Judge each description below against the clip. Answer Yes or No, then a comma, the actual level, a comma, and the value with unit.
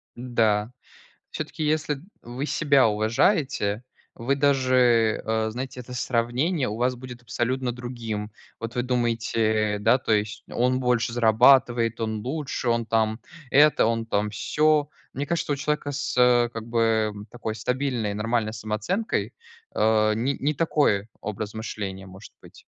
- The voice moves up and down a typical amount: Yes, average, 3.0 semitones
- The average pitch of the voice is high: No, low, 120 Hz